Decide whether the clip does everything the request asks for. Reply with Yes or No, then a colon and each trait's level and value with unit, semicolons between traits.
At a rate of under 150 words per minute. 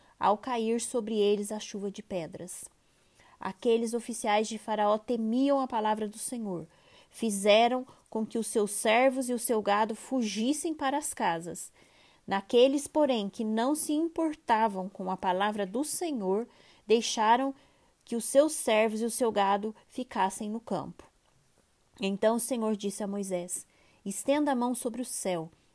No: average, 155 wpm